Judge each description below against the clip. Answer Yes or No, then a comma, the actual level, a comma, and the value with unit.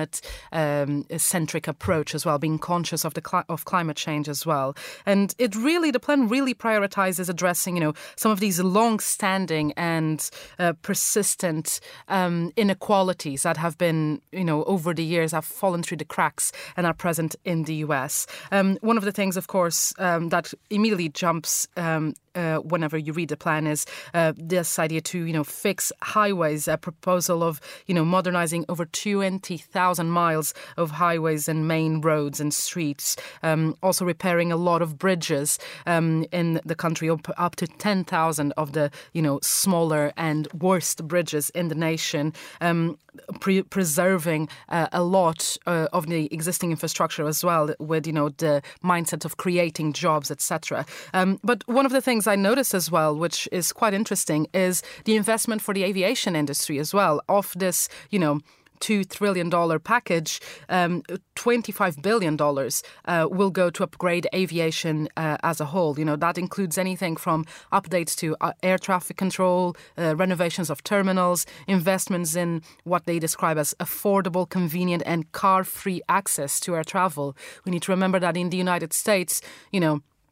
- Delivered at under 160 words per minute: No, average, 175 wpm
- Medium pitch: Yes, medium, 170 Hz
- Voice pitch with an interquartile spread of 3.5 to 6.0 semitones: No, average, 2.9 semitones